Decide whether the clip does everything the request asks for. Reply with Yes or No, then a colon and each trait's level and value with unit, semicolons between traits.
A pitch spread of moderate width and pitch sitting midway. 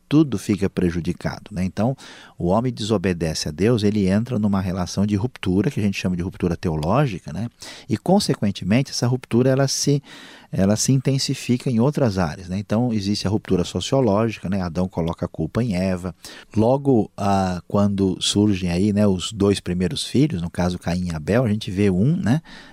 No: average, 4.8 semitones; low, 100 Hz